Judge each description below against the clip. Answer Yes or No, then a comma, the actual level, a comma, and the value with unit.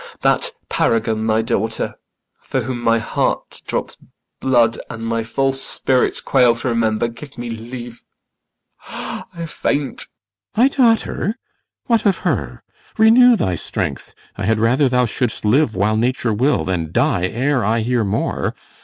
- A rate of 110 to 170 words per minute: Yes, average, 150 wpm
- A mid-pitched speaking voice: No, low, 120 Hz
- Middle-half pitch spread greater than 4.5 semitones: No, average, 3.4 semitones